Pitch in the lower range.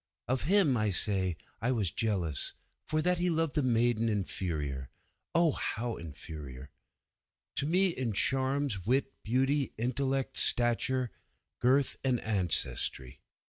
Yes: low, 120 Hz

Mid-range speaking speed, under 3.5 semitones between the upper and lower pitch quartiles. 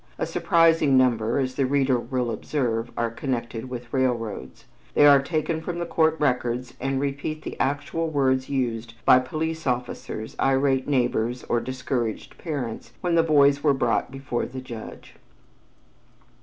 Yes: average, 150 wpm; average, 3.1 semitones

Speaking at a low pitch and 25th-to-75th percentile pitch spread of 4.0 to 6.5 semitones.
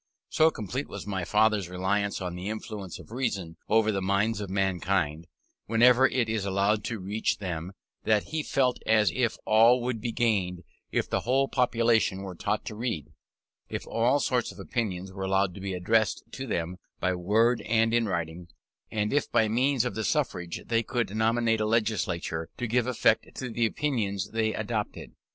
No: low, 110 Hz; average, 3.6 semitones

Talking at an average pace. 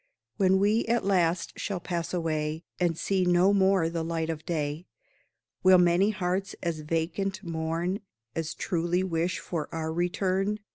Yes: average, 150 wpm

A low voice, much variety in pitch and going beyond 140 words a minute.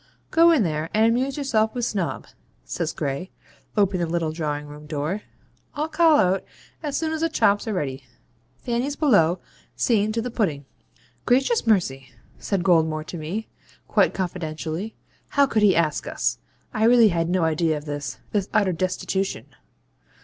No: high, 190 Hz; wide, 6.7 semitones; average, 165 wpm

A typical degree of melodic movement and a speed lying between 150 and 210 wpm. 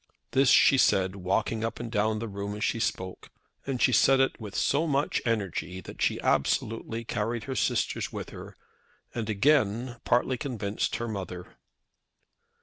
Yes: average, 3.8 semitones; average, 160 wpm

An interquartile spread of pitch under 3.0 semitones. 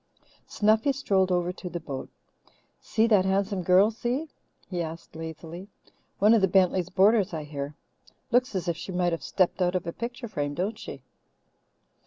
No: average, 3.8 semitones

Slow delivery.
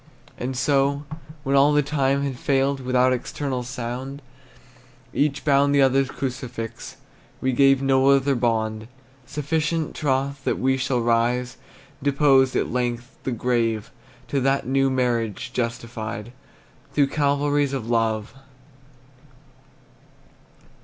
Yes: slow, 120 wpm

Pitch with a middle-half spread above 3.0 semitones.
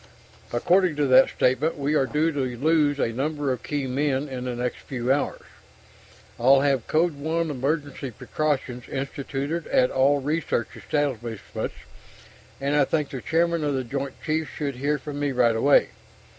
No: narrow, 2.6 semitones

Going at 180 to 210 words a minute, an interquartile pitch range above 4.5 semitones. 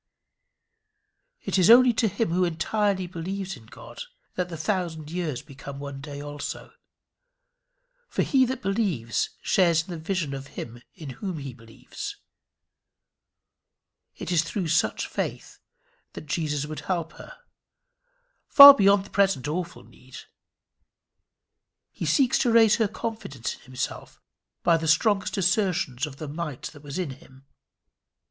No: average, 140 wpm; average, 5.2 semitones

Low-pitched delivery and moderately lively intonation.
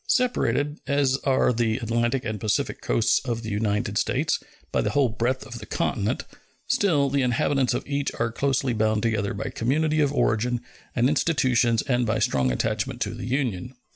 Yes: low, 120 Hz; average, 3.6 semitones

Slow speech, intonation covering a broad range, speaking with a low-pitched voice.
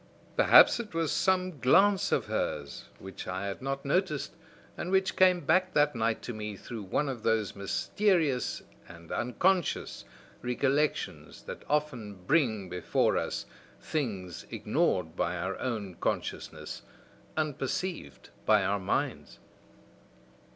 Yes: slow, 125 wpm; wide, 8.5 semitones; low, 125 Hz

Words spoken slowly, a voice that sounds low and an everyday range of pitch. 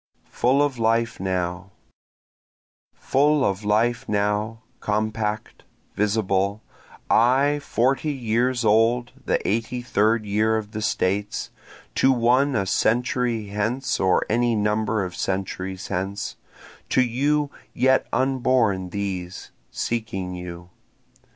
Yes: slow, 110 wpm; low, 110 Hz; average, 3.6 semitones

